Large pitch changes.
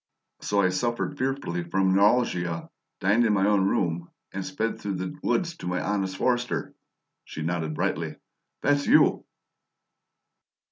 No: average, 4.9 semitones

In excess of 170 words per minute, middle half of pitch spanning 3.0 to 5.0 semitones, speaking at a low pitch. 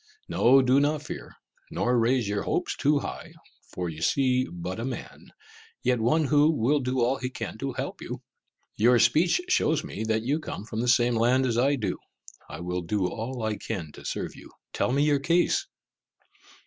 Yes: average, 195 wpm; average, 4.2 semitones; low, 125 Hz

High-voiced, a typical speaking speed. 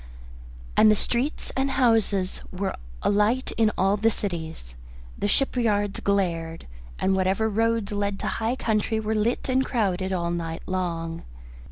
Yes: high, 205 Hz; average, 145 wpm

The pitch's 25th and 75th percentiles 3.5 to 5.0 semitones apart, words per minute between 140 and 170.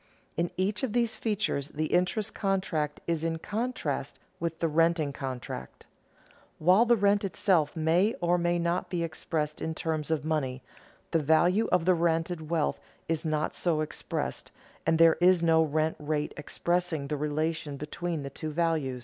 No: narrow, 2.6 semitones; average, 165 wpm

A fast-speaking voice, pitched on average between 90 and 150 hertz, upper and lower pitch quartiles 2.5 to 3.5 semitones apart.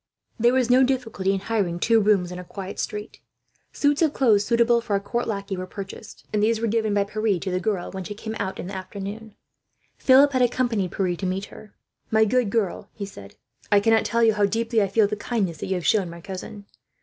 No: fast, 235 wpm; high, 210 Hz; average, 3.0 semitones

